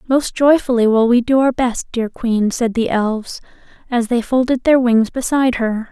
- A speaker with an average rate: Yes, average, 195 wpm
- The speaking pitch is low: No, high, 240 Hz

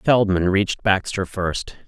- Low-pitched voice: Yes, very low, 95 Hz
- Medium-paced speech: No, slow, 130 wpm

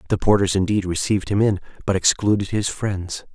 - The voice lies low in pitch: Yes, low, 100 Hz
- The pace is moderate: Yes, average, 180 wpm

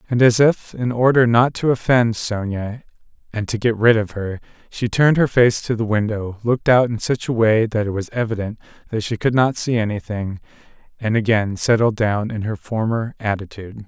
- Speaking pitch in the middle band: No, low, 110 Hz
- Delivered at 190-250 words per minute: Yes, average, 200 wpm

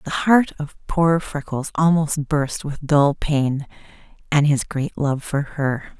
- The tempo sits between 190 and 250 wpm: No, average, 160 wpm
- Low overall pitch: No, medium, 150 Hz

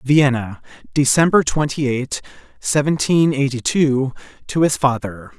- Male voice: Yes, male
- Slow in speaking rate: Yes, slow, 110 wpm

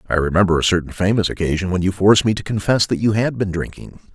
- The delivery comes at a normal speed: No, fast, 245 wpm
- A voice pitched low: Yes, very low, 95 Hz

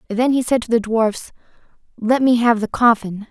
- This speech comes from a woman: Yes, female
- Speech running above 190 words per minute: Yes, average, 200 wpm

